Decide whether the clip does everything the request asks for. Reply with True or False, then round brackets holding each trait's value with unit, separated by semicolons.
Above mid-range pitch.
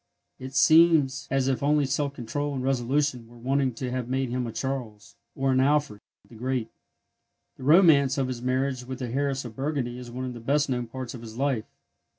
False (130 Hz)